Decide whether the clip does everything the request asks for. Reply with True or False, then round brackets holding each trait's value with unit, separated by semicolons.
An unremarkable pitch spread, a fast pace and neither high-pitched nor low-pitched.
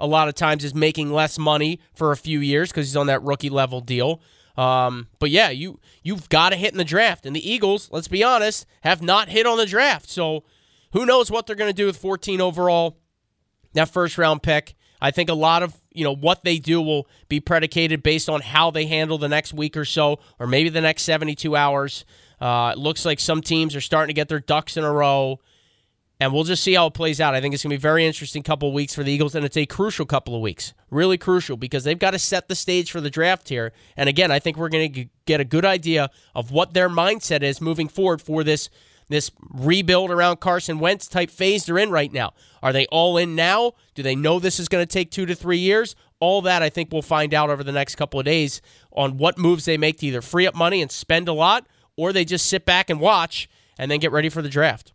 True (3.5 semitones; 255 wpm; 155 Hz)